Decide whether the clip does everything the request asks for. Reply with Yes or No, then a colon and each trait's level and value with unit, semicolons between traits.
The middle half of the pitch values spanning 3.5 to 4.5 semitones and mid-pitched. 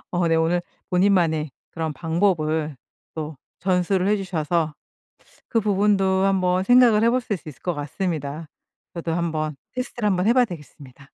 Yes: average, 3.8 semitones; medium, 175 Hz